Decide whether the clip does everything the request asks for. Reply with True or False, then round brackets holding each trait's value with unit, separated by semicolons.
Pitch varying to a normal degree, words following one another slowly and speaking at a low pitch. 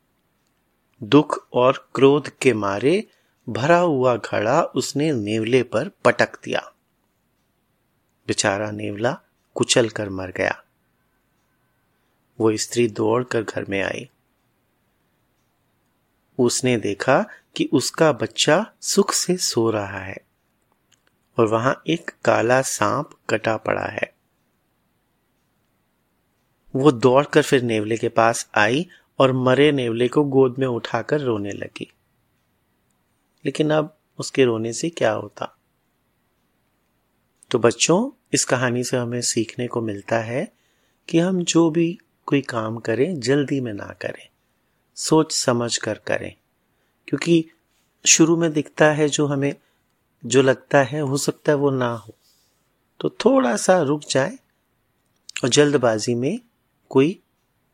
False (4.4 semitones; 120 wpm; 130 Hz)